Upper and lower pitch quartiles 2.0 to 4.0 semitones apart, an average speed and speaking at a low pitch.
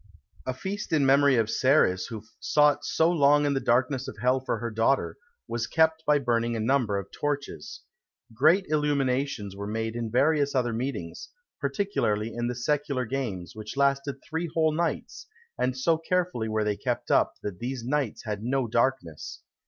No: average, 4.5 semitones; average, 175 wpm; low, 130 Hz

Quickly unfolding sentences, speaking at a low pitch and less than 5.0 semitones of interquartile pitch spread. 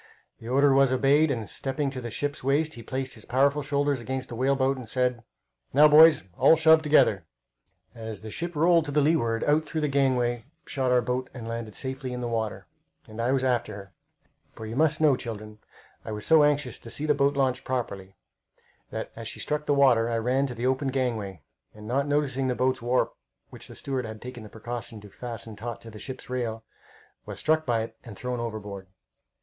Yes: fast, 210 wpm; low, 130 Hz; average, 3.6 semitones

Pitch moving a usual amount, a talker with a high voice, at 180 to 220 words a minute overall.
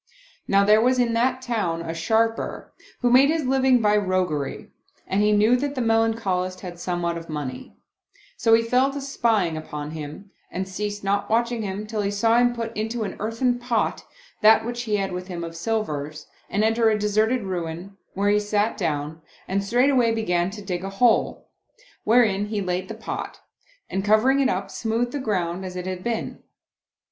Yes: average, 4.0 semitones; high, 210 Hz; average, 190 wpm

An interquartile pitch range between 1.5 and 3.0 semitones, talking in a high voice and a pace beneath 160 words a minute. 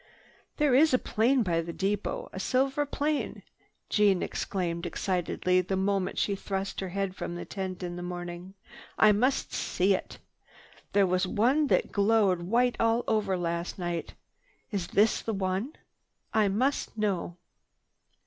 No: average, 3.8 semitones; high, 195 Hz; average, 150 wpm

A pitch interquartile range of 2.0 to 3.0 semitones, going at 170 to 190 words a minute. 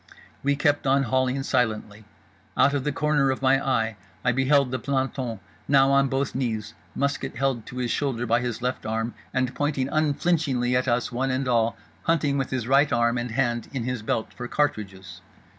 Yes: narrow, 2.6 semitones; average, 180 wpm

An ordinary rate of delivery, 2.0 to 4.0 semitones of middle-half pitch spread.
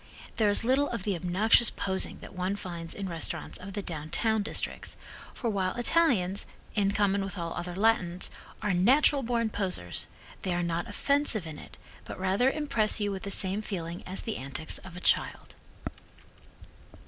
Yes: average, 170 wpm; average, 3.7 semitones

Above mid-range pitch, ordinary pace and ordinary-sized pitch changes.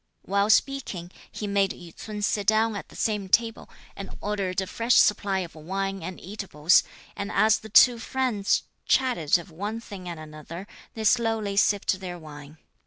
Yes: high, 200 Hz; average, 175 wpm; average, 3.3 semitones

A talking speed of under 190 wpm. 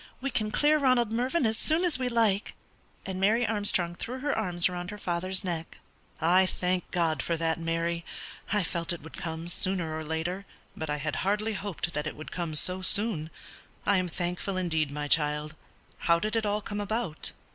No: average, 195 wpm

